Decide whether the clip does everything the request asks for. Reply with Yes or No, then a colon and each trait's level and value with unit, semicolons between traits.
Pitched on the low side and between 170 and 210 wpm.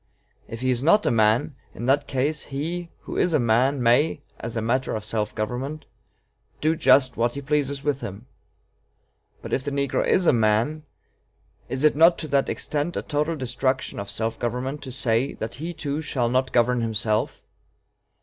Yes: low, 130 Hz; average, 185 wpm